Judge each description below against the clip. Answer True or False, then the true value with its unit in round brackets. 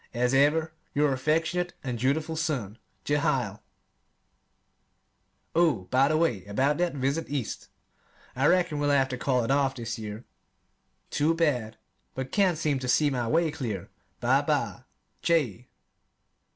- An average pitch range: True (4.1 semitones)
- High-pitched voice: False (140 Hz)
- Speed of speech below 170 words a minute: True (140 wpm)